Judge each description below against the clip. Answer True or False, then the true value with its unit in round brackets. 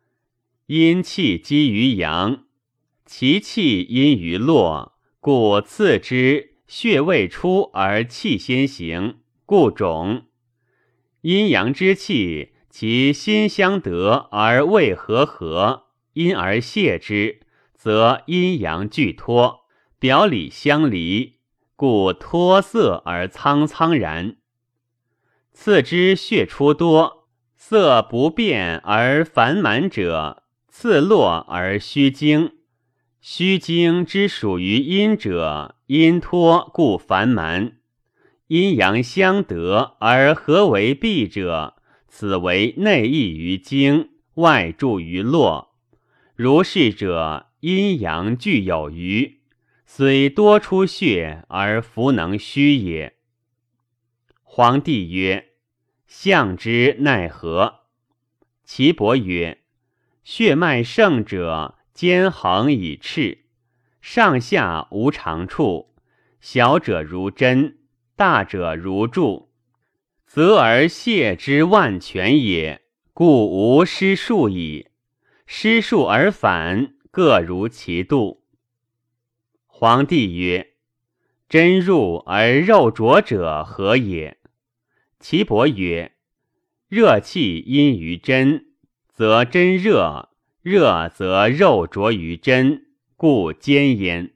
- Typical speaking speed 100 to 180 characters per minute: True (130 characters per minute)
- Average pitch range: False (7.6 semitones)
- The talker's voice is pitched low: True (125 Hz)